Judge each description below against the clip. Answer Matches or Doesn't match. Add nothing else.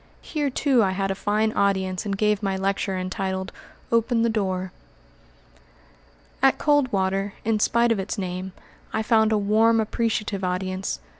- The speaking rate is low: Doesn't match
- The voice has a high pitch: Matches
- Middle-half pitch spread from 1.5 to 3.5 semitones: Matches